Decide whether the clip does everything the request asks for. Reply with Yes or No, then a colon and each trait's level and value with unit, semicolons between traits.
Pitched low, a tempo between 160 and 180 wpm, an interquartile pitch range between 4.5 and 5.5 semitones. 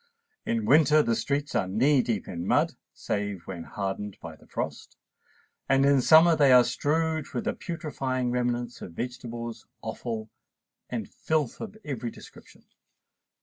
No: low, 125 Hz; average, 145 wpm; average, 5.1 semitones